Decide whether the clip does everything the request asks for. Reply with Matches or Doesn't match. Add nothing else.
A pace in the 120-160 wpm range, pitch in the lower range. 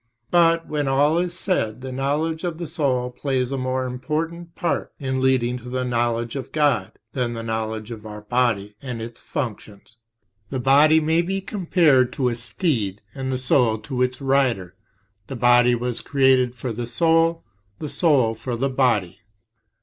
Doesn't match